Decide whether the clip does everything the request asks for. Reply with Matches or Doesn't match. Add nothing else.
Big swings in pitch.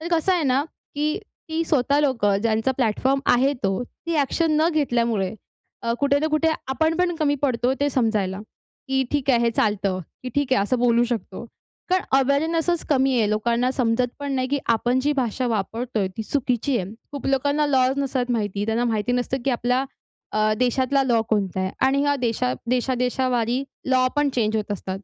Doesn't match